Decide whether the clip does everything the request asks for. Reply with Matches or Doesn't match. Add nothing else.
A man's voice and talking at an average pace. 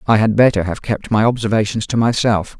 Doesn't match